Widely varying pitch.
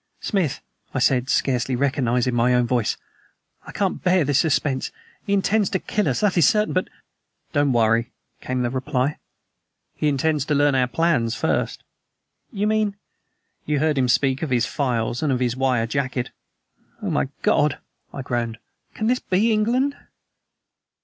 Yes: wide, 6.6 semitones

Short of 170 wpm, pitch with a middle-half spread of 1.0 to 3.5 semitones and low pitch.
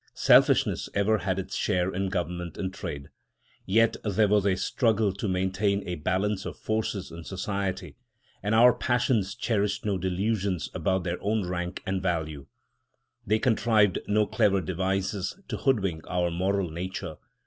Yes: average, 150 wpm; narrow, 2.5 semitones; very low, 95 Hz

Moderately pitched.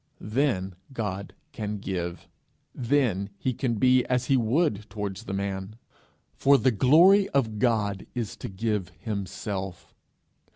No: low, 110 Hz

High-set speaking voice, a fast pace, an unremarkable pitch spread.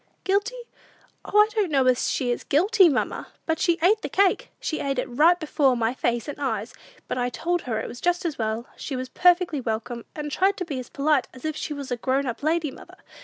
No: very high, 290 Hz; fast, 235 wpm; wide, 5.9 semitones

